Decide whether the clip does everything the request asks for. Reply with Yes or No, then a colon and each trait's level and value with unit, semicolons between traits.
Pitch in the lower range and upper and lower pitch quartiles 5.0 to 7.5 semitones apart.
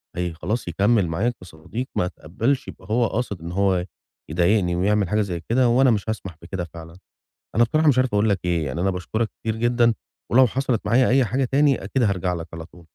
Yes: low, 105 Hz; average, 5.3 semitones